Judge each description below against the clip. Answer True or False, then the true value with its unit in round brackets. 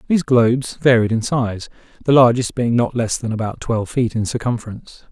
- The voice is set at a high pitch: False (120 Hz)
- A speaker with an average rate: True (190 wpm)